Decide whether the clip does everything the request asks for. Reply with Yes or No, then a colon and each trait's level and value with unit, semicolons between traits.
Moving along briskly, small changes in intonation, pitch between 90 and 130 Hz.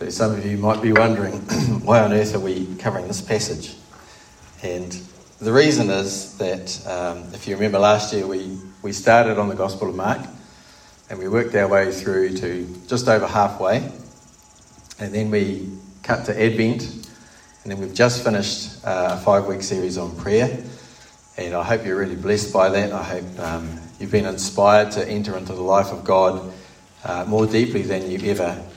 No: average, 180 wpm; narrow, 2.3 semitones; low, 100 Hz